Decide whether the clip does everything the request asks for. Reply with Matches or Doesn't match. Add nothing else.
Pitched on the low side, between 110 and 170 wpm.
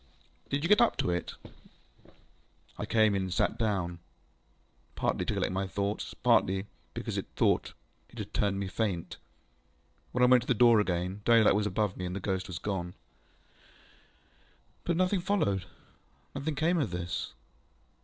Matches